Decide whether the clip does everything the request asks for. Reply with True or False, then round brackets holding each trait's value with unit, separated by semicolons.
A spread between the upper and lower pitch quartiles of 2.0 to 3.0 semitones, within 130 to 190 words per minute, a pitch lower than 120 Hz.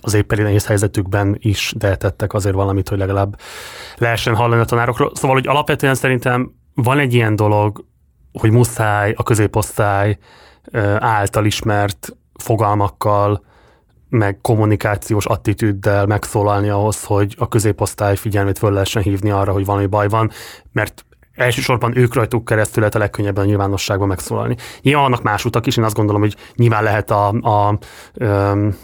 True (2.5 semitones; 150 wpm; 105 Hz)